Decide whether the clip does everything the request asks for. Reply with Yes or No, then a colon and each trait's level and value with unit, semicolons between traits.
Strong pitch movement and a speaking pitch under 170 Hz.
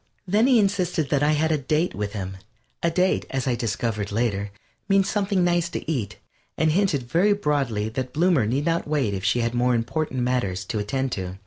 Yes: wide, 6.9 semitones; low, 135 Hz